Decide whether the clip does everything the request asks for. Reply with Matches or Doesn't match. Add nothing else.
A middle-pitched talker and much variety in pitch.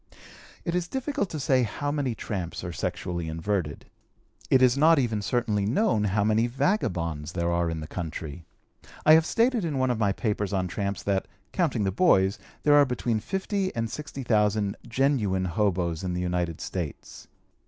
Doesn't match